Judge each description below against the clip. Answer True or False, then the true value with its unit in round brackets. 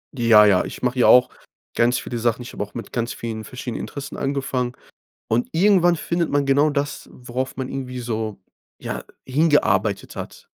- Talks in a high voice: False (125 Hz)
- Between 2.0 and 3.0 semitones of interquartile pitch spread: False (3.5 semitones)